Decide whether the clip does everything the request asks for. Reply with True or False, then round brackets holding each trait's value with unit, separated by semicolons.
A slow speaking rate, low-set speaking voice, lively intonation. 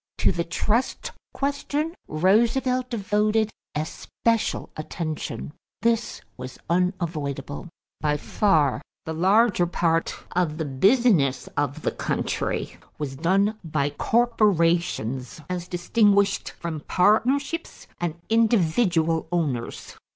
False (100 wpm; 175 Hz; 6.2 semitones)